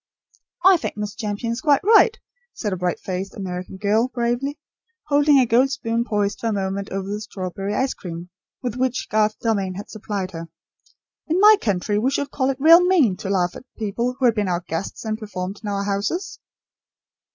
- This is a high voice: Yes, high, 215 Hz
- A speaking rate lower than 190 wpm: No, average, 195 wpm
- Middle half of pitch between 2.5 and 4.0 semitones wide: No, average, 4.9 semitones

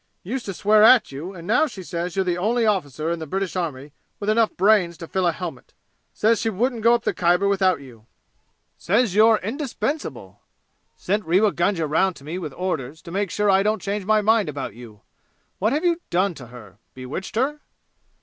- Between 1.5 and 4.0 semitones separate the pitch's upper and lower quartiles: No, average, 4.6 semitones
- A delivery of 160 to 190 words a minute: No, average, 200 wpm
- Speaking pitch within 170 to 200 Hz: Yes, high, 190 Hz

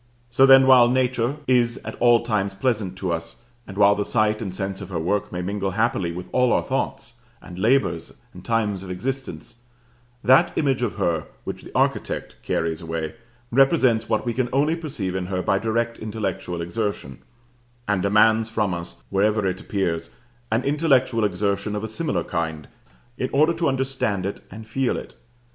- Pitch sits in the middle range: No, low, 110 Hz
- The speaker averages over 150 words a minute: Yes, average, 180 wpm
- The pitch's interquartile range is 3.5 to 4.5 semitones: No, average, 4.9 semitones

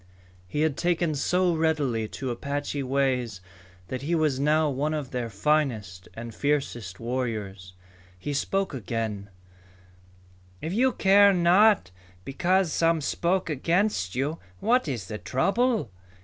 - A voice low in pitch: No, medium, 145 Hz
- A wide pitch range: Yes, wide, 6.4 semitones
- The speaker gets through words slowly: Yes, slow, 130 wpm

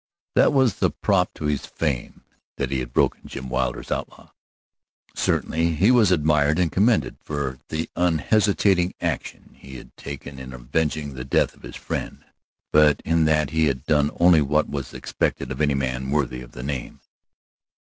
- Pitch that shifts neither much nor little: Yes, average, 3.7 semitones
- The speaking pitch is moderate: No, very low, 75 Hz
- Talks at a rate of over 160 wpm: Yes, average, 170 wpm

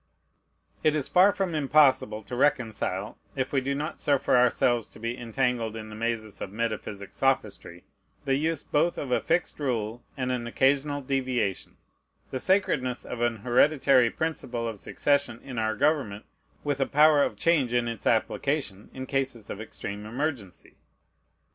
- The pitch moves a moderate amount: Yes, average, 4.1 semitones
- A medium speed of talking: Yes, average, 160 wpm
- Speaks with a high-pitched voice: No, low, 125 Hz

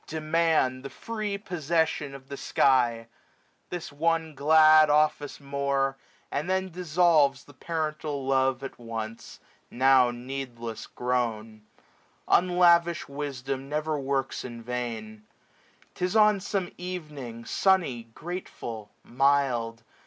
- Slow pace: Yes, slow, 110 wpm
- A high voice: No, medium, 140 Hz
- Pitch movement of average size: Yes, average, 4.7 semitones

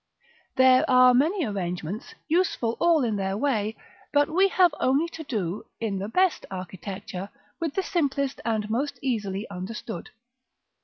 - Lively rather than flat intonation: Yes, wide, 6.4 semitones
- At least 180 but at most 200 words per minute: No, average, 145 wpm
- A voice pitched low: No, high, 235 Hz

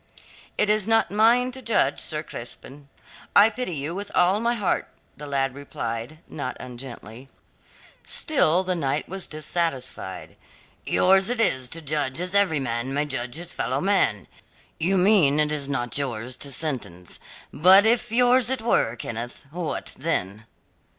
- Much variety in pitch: Yes, wide, 7.1 semitones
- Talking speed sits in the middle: Yes, average, 150 wpm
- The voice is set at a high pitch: No, medium, 155 Hz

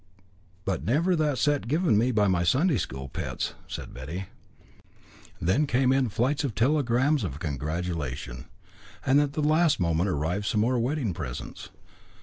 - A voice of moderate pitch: No, low, 115 Hz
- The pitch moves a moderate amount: No, wide, 8.9 semitones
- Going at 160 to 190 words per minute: No, average, 150 wpm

